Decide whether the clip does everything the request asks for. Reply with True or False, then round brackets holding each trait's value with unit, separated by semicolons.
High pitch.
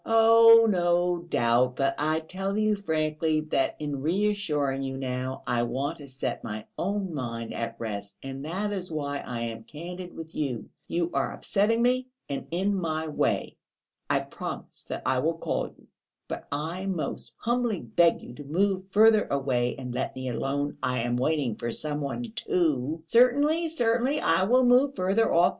False (160 Hz)